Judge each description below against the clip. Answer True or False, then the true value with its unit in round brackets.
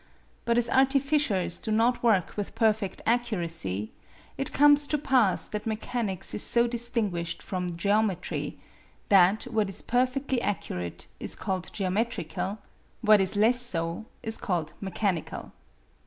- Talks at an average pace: False (130 wpm)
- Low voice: False (215 Hz)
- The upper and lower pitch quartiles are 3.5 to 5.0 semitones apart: True (4.5 semitones)